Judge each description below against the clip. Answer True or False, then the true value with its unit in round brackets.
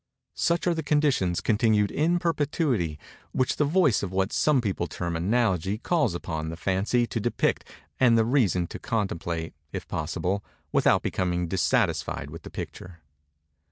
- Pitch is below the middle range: True (105 Hz)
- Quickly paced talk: False (155 wpm)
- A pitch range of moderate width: False (7.8 semitones)